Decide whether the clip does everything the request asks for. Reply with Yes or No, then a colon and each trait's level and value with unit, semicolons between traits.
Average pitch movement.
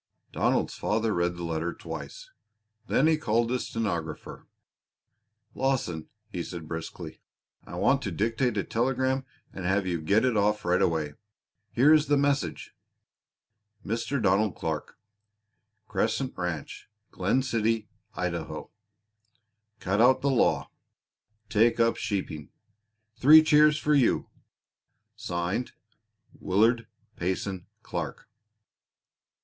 No: wide, 6.5 semitones